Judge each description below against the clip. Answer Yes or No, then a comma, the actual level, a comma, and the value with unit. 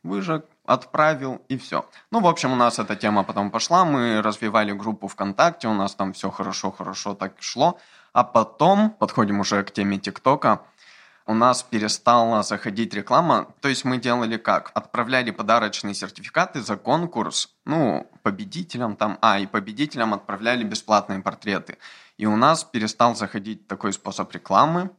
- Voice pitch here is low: Yes, low, 110 Hz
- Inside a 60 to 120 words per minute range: No, average, 150 wpm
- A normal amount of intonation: Yes, average, 3.9 semitones